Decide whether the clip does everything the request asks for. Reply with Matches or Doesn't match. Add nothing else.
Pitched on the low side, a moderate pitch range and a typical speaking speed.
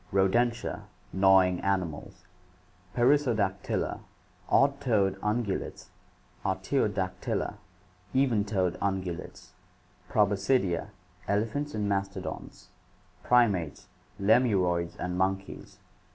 Doesn't match